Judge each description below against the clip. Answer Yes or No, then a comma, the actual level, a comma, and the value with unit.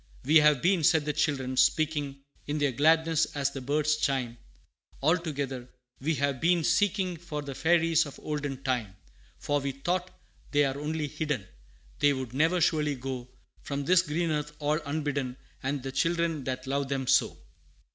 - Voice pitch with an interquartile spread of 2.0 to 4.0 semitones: Yes, average, 2.8 semitones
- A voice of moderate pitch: Yes, medium, 145 Hz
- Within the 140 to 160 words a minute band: No, average, 170 wpm